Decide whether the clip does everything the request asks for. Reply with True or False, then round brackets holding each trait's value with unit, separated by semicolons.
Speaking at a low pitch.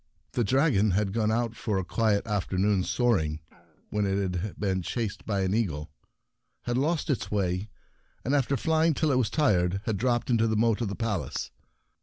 True (105 Hz)